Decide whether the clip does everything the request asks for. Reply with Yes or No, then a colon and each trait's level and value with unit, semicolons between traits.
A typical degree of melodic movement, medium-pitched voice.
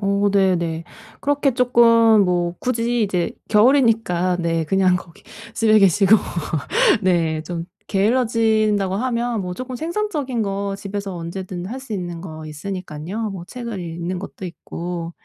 No: average, 4.6 semitones; high, 195 Hz